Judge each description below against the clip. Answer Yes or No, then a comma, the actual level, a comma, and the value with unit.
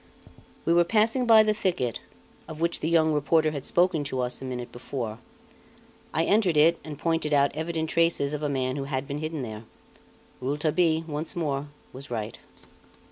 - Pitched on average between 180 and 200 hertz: No, medium, 155 Hz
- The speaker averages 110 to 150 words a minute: No, average, 180 wpm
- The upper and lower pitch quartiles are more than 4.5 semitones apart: No, average, 3.6 semitones